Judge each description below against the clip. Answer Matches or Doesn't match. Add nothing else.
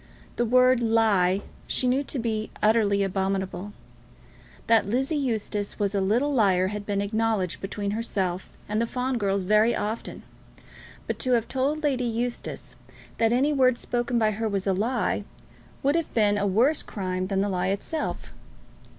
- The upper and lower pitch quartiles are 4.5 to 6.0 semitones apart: Doesn't match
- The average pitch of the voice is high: Matches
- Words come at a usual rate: Matches